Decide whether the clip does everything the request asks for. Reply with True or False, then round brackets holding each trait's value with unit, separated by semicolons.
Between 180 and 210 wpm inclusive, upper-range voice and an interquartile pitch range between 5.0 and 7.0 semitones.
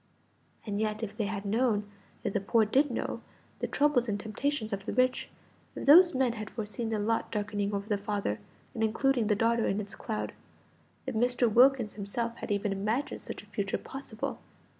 False (190 wpm; 220 Hz; 3.0 semitones)